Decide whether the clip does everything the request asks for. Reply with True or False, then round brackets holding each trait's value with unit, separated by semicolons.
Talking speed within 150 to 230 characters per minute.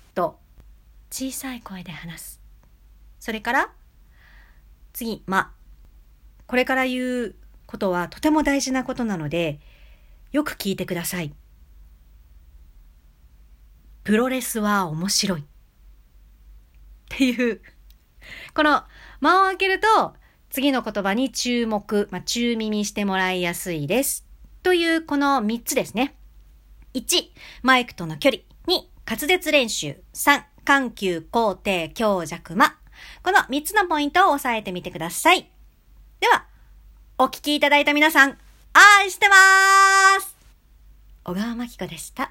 True (225 characters per minute)